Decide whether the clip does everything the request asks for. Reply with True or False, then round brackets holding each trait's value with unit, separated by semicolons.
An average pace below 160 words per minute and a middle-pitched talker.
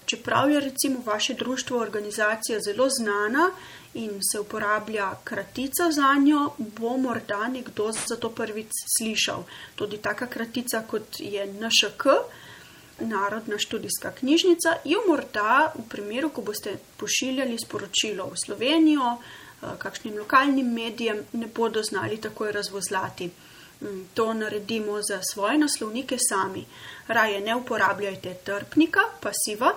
False (120 wpm; 225 Hz)